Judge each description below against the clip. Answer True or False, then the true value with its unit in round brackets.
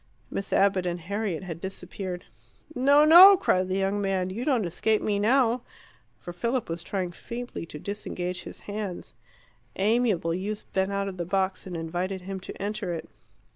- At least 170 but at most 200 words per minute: True (175 wpm)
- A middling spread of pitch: True (3.1 semitones)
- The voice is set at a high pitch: True (195 Hz)